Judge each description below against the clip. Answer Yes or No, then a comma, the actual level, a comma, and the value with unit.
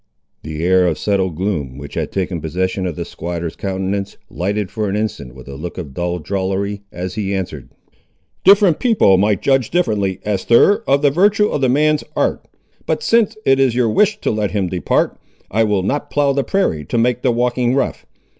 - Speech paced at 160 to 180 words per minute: No, average, 195 wpm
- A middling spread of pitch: No, wide, 6.5 semitones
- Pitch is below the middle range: Yes, low, 100 Hz